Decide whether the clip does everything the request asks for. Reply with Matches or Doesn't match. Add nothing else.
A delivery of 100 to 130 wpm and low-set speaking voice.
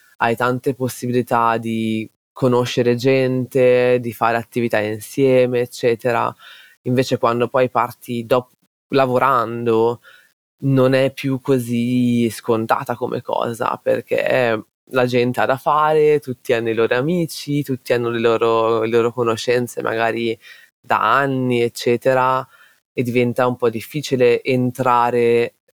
Matches